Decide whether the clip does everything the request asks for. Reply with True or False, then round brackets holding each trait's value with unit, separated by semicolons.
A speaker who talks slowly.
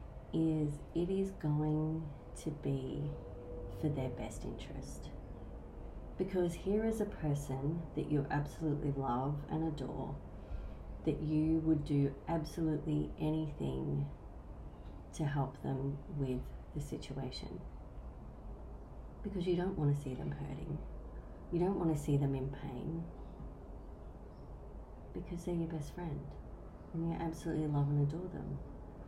True (125 wpm)